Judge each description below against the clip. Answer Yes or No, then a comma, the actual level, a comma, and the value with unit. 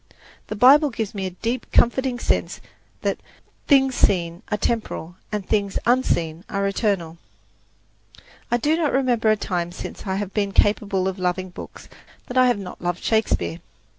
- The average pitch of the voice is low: No, high, 205 Hz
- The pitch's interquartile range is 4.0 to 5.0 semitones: Yes, average, 4.7 semitones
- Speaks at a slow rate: No, average, 165 wpm